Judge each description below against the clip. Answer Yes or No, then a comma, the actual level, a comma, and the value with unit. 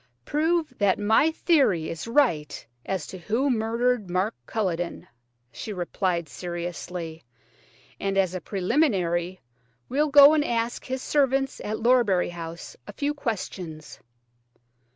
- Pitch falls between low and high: No, high, 205 Hz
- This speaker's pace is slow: Yes, slow, 125 wpm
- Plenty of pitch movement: Yes, wide, 6.9 semitones